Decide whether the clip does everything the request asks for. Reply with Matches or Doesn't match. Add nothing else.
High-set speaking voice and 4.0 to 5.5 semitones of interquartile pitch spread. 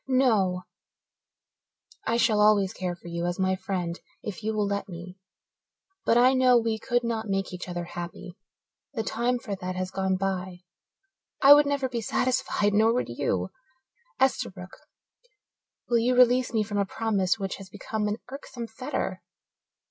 Matches